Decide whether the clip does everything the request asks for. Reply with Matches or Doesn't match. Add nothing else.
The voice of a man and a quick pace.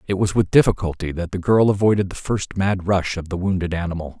Matches